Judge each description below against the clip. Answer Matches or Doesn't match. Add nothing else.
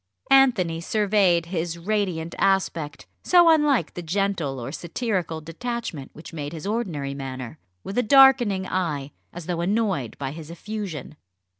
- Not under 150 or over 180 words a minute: Doesn't match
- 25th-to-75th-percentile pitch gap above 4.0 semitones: Matches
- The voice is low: Doesn't match